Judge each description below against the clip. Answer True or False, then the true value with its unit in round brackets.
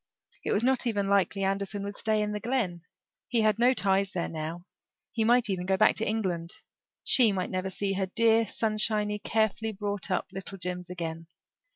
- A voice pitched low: False (200 Hz)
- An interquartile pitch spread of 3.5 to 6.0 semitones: False (2.8 semitones)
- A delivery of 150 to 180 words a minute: False (190 wpm)